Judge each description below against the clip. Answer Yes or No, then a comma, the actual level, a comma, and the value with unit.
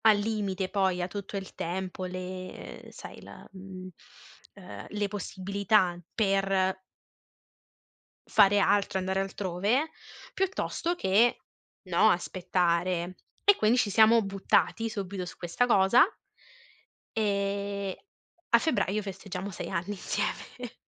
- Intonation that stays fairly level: Yes, narrow, 2.2 semitones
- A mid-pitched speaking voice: No, high, 195 Hz